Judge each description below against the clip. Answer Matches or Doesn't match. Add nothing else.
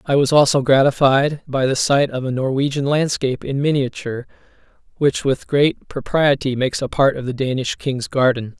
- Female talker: Doesn't match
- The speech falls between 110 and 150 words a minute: Doesn't match